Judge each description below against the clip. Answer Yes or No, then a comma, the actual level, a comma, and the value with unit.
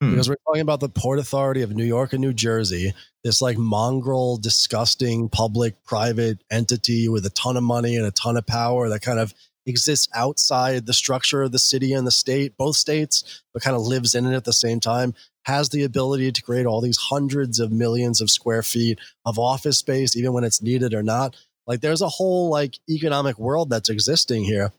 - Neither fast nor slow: No, fast, 210 wpm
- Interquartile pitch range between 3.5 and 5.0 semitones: No, average, 2.7 semitones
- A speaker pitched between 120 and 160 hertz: Yes, low, 125 Hz